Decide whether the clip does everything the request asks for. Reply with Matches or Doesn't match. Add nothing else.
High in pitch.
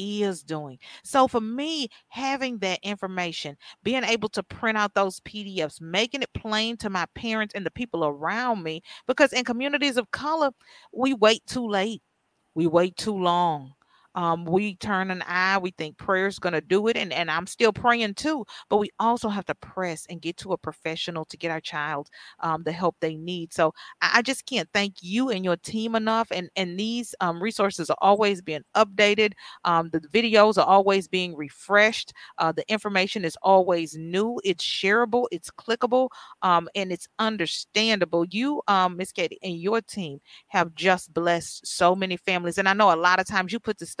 Matches